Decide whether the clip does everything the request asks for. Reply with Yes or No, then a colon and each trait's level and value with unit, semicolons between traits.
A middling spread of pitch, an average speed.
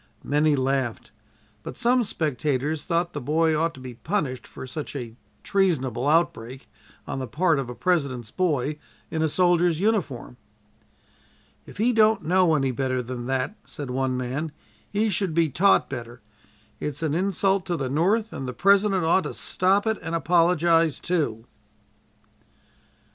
No: wide, 5.7 semitones; average, 155 wpm